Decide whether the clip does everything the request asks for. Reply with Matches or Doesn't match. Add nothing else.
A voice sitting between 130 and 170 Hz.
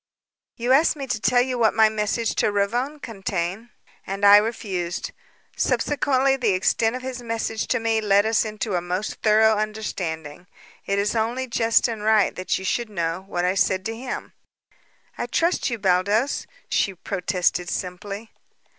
Doesn't match